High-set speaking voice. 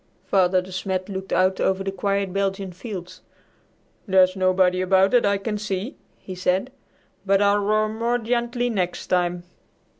Yes: high, 195 Hz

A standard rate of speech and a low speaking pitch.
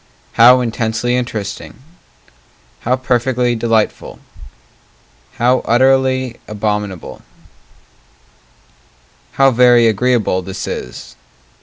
No: slow, 70 wpm; low, 120 Hz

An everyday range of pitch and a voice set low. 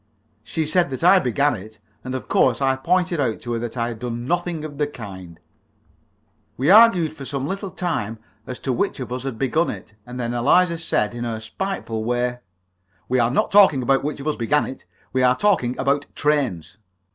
Yes: average, 4.8 semitones; low, 130 Hz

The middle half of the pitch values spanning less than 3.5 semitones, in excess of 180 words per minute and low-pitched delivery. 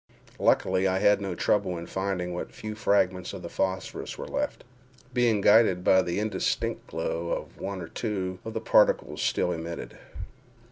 No: average, 3.0 semitones; average, 155 wpm; very low, 95 Hz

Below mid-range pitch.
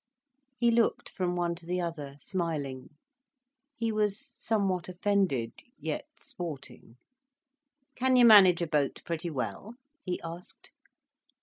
No: medium, 180 Hz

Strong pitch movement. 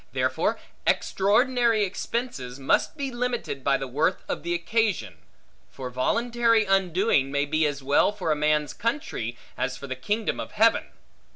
Yes: wide, 8.7 semitones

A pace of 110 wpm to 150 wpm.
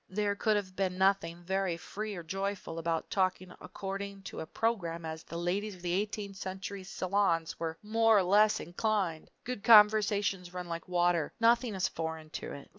No: average, 180 wpm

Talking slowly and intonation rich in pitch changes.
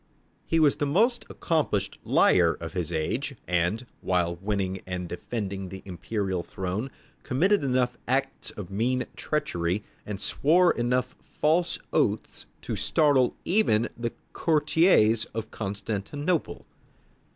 Yes: slow, 120 wpm; wide, 7.2 semitones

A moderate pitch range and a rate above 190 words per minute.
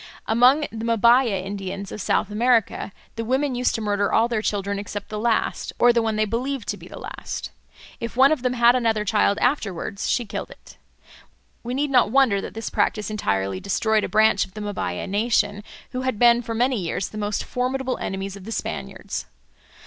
Yes: average, 3.2 semitones; average, 200 wpm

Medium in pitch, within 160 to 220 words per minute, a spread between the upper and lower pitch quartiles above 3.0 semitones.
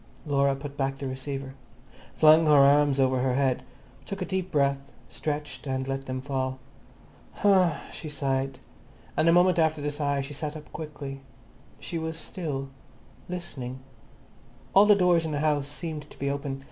No: medium, 145 Hz; average, 170 wpm; average, 2.7 semitones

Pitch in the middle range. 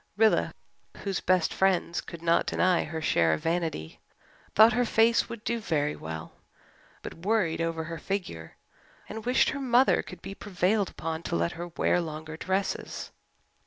Yes: medium, 175 Hz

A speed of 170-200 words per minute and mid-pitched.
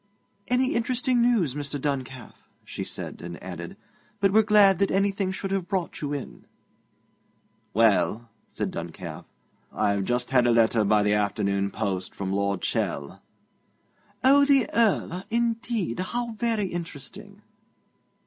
No: slow, 135 wpm; medium, 145 Hz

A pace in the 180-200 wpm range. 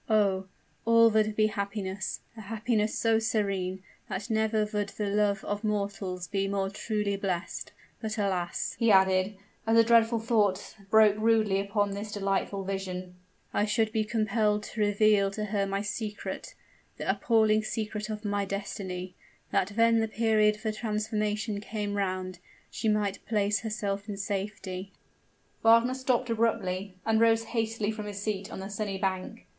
No: average, 160 wpm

